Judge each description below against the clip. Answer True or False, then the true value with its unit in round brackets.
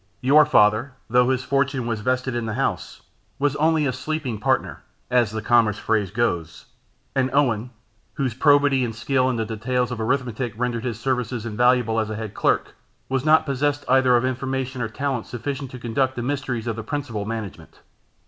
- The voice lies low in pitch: True (125 Hz)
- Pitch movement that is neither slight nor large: True (3.0 semitones)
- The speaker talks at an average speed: True (185 wpm)